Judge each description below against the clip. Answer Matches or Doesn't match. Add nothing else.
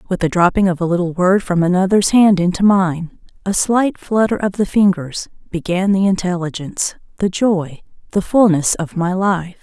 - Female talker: Matches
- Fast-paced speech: Doesn't match